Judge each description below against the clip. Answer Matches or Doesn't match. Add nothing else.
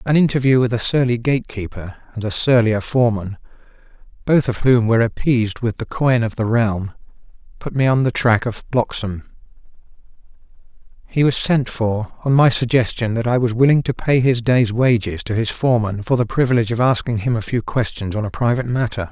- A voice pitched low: Matches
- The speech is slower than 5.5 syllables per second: Doesn't match